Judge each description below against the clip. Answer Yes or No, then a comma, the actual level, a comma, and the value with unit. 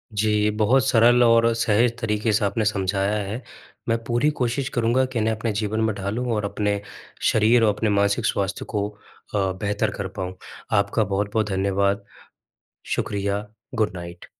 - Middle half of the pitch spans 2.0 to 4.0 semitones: Yes, narrow, 2.4 semitones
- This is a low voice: Yes, low, 105 Hz